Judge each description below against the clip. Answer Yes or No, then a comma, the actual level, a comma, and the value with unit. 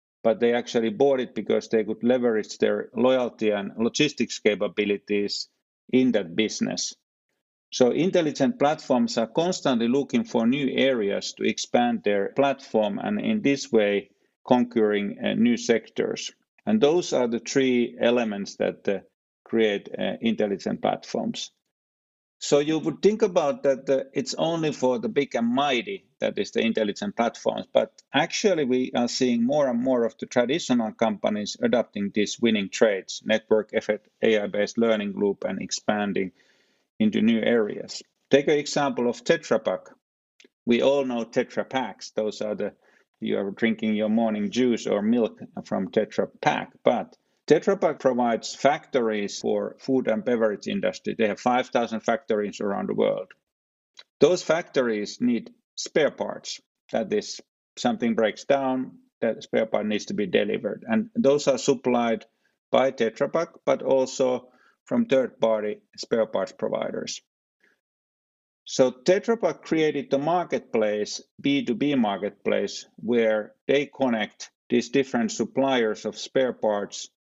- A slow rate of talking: No, average, 145 wpm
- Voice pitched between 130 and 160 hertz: No, low, 120 Hz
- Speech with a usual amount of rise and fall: Yes, average, 4.2 semitones